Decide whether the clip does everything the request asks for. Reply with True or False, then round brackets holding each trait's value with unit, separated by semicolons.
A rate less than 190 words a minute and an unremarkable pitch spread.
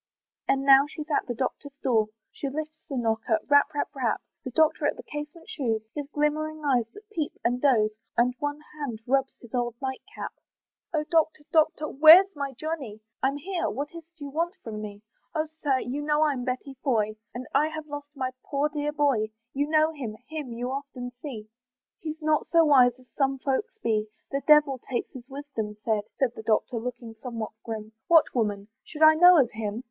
False (195 wpm; 4.0 semitones)